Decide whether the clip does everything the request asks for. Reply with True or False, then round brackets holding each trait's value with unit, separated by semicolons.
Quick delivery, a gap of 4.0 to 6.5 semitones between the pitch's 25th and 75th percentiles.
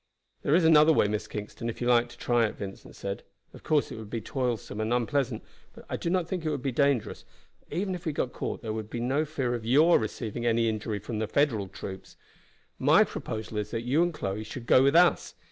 True (240 wpm; 5.2 semitones)